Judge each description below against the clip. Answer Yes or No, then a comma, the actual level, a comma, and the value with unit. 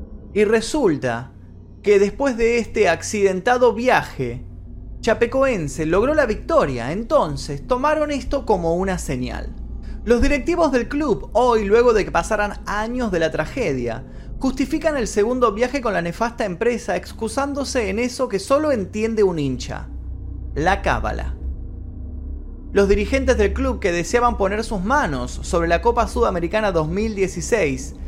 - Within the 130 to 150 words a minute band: Yes, average, 135 wpm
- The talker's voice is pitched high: Yes, high, 205 Hz